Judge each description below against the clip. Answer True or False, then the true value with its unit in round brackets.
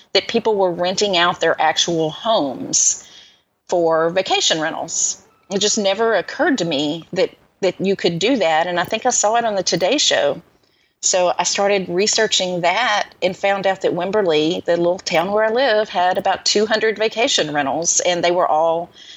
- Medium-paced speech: True (180 wpm)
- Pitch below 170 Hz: False (190 Hz)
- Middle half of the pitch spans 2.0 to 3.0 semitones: False (3.6 semitones)